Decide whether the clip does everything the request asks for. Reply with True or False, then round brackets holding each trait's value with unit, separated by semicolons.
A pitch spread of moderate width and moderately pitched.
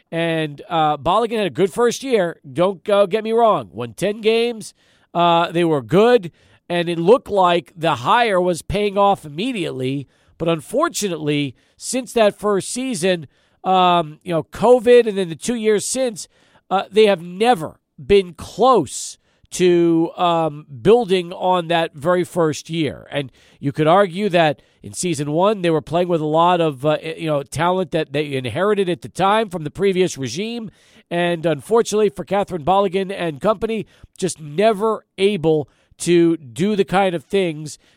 True (4.2 semitones; 180 Hz)